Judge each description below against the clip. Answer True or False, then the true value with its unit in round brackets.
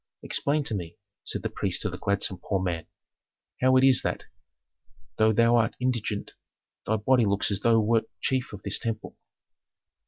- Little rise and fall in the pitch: False (3.7 semitones)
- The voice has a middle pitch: False (110 Hz)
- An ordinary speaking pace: True (180 wpm)